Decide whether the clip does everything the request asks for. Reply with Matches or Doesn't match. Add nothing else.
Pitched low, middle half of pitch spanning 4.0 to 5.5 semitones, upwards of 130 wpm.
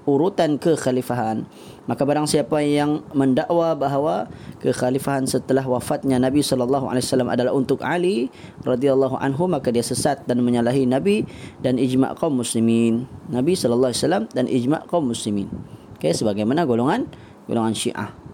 Doesn't match